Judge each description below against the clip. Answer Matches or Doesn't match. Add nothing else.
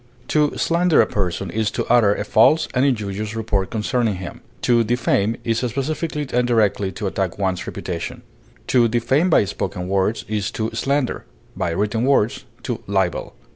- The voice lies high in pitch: Doesn't match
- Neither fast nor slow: Matches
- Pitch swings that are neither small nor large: Matches